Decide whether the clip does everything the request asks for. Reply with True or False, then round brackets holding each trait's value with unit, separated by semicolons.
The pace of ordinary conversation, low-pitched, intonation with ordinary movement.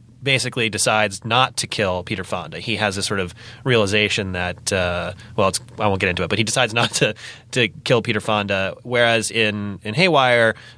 True (195 wpm; 110 Hz; 3.0 semitones)